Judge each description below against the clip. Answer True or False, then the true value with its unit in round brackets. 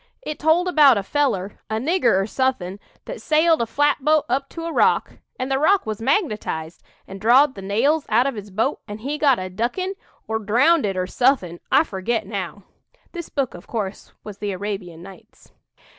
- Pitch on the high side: True (230 Hz)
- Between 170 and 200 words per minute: True (190 wpm)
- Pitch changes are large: True (6.7 semitones)